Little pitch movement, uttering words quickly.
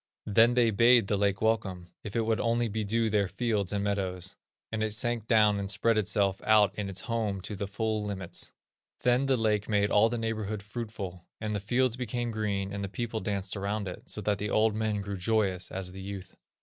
Yes: narrow, 2.2 semitones; fast, 215 wpm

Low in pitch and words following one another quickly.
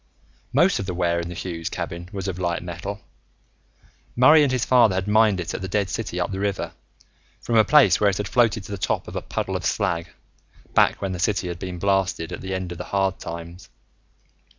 Yes: very low, 95 Hz; fast, 225 wpm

